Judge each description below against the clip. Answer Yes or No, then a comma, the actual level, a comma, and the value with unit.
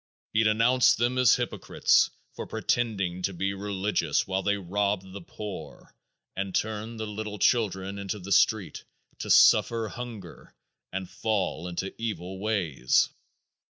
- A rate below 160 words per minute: Yes, slow, 135 wpm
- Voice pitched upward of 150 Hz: No, low, 100 Hz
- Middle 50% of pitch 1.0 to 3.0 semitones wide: Yes, narrow, 2.6 semitones